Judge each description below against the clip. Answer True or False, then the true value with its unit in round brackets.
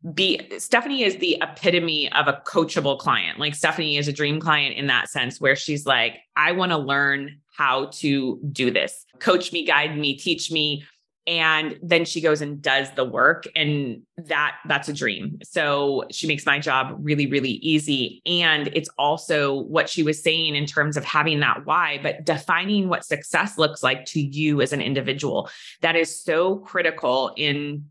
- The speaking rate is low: False (185 wpm)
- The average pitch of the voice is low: False (150 Hz)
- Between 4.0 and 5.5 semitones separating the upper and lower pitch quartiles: False (2.6 semitones)